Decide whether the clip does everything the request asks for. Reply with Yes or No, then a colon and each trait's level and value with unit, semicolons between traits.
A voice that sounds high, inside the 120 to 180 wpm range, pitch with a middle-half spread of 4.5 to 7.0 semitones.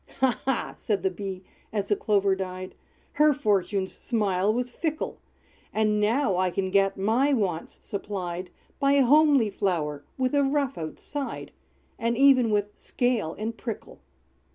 Yes: high, 210 Hz; average, 150 wpm; average, 5.2 semitones